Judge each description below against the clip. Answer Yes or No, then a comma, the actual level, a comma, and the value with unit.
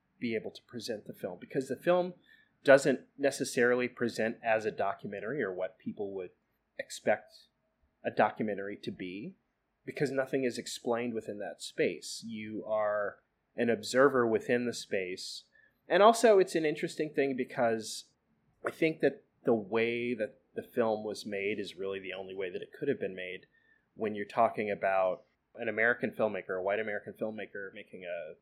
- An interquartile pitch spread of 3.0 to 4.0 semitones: No, average, 4.4 semitones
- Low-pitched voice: Yes, low, 120 Hz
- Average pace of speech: Yes, average, 165 wpm